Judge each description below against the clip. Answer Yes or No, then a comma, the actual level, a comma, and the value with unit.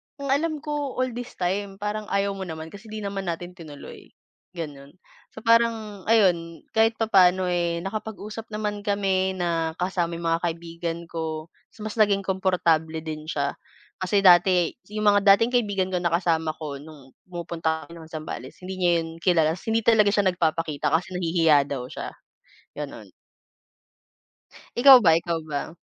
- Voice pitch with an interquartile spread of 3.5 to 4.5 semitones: Yes, average, 4.1 semitones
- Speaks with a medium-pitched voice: Yes, medium, 180 Hz